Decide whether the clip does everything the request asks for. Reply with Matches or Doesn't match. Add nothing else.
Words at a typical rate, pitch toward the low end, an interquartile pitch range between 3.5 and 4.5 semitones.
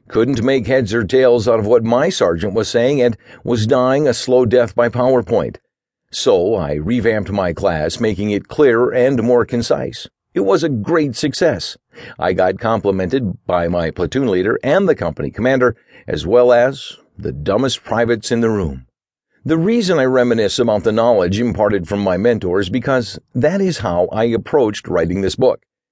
Matches